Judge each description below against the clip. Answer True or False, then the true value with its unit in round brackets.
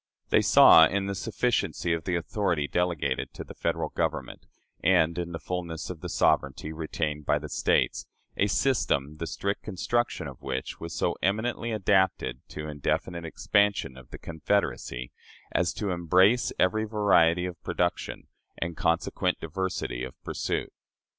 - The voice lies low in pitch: True (85 Hz)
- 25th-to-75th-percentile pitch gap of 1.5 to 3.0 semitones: False (4.0 semitones)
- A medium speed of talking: True (150 wpm)